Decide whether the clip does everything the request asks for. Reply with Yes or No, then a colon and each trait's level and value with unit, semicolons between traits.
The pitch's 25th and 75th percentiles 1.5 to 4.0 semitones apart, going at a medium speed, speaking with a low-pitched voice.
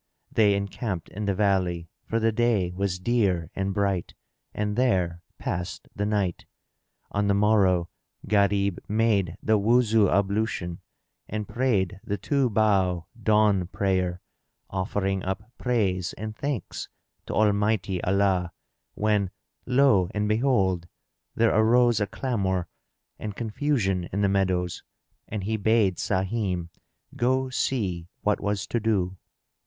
No: average, 2.9 semitones; slow, 125 wpm; low, 100 Hz